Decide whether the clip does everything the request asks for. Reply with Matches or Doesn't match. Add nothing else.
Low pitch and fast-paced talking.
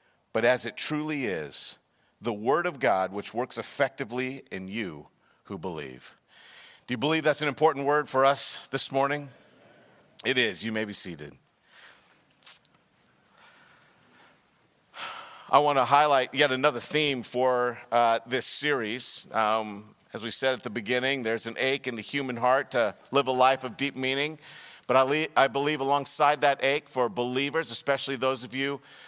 Doesn't match